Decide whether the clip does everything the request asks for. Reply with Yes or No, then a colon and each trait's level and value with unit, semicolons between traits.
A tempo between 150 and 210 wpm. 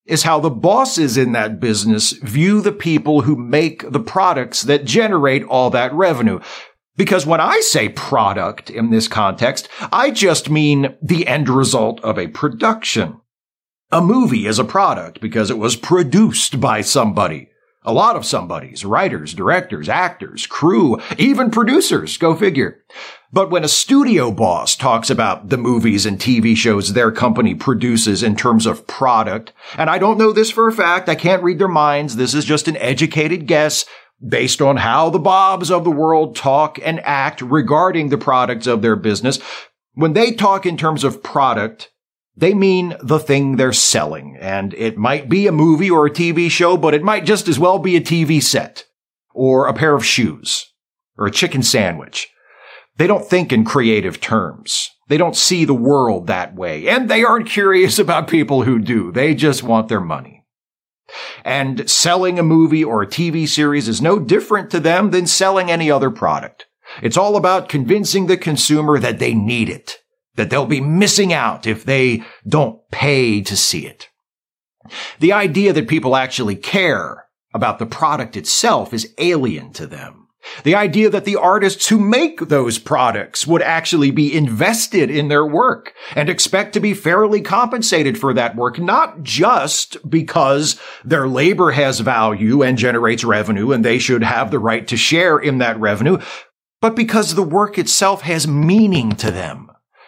Yes: average, 175 wpm